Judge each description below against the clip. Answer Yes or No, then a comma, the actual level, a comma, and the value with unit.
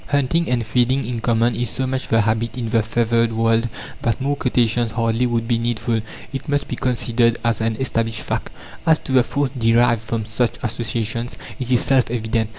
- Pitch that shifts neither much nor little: No, narrow, 1.9 semitones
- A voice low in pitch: Yes, low, 115 Hz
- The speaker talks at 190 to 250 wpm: Yes, average, 195 wpm